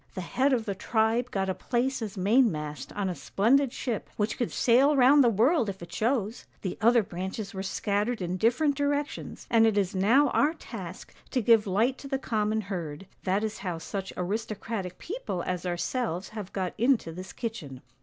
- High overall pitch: Yes, high, 215 Hz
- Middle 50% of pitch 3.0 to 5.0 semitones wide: Yes, average, 4.6 semitones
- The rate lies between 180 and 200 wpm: Yes, average, 190 wpm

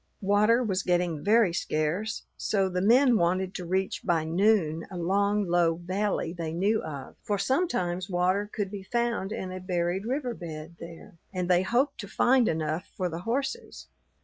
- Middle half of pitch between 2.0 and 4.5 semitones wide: Yes, average, 3.6 semitones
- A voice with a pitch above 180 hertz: Yes, high, 190 Hz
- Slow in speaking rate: No, average, 175 wpm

